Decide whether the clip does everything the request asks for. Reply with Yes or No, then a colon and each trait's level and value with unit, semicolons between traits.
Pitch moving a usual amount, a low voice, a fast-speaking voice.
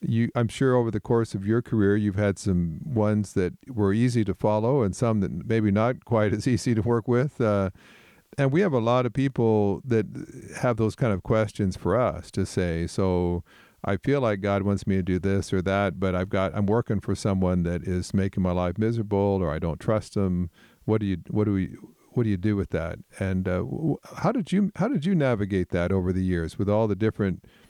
Yes: average, 3.7 semitones; low, 105 Hz; fast, 230 wpm